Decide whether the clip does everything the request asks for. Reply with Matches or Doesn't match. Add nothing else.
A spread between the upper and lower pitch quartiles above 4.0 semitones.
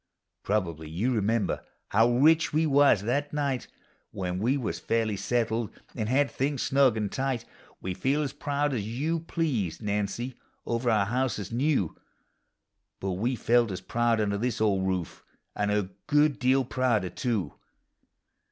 Matches